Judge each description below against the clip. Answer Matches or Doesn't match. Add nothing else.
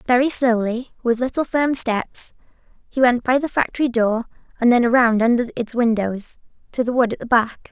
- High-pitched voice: Matches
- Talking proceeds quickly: Doesn't match